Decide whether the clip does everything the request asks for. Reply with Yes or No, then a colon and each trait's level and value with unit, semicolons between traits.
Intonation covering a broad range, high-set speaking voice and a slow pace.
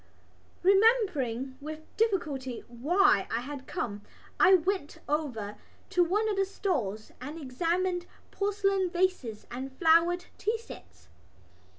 Yes: wide, 6.8 semitones; very high, 330 Hz; slow, 115 wpm